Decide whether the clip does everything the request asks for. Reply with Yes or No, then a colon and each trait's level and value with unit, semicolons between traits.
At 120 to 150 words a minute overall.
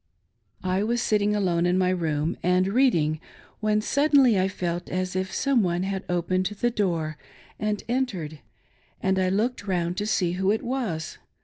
No: average, 170 wpm